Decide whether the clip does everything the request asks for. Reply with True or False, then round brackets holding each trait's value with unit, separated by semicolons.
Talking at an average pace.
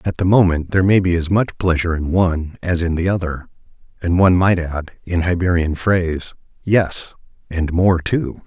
True (185 wpm)